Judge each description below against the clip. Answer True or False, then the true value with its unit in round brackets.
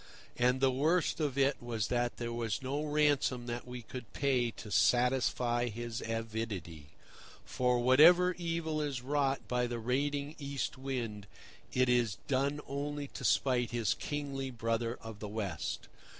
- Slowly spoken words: False (150 wpm)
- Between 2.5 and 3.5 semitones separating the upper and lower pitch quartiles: True (3.2 semitones)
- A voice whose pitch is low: True (125 Hz)